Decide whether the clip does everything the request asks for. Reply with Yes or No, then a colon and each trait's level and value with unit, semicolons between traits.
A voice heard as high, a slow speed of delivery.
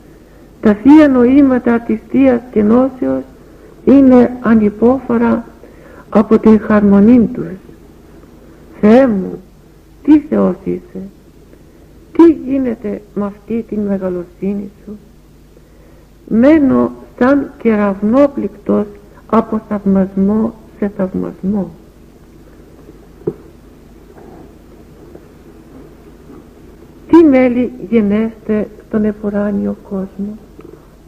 Yes: high, 210 Hz; slow, 75 wpm